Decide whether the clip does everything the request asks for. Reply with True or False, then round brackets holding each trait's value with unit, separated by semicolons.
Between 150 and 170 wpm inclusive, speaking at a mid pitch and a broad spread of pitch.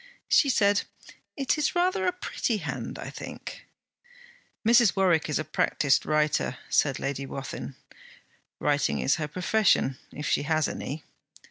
False (140 wpm; 160 Hz; 8.3 semitones)